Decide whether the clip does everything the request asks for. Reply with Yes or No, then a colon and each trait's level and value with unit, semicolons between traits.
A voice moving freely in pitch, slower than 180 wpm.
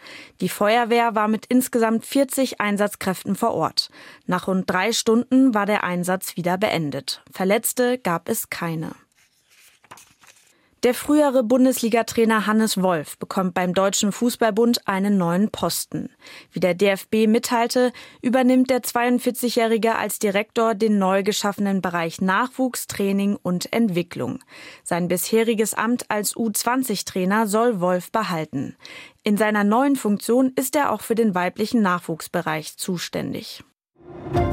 No: average, 4.0 semitones; slow, 125 wpm